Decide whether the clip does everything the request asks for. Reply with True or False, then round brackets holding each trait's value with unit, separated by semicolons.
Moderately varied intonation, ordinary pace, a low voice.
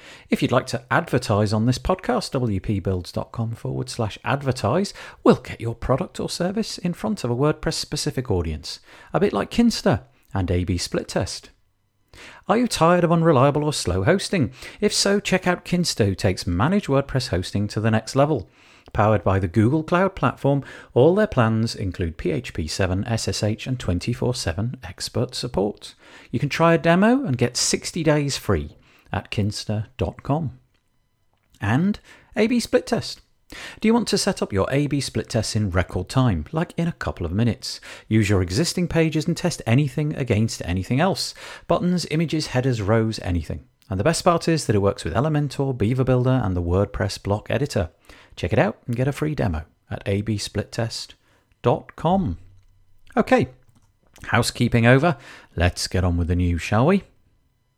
False (7.3 semitones; 165 wpm; 120 Hz)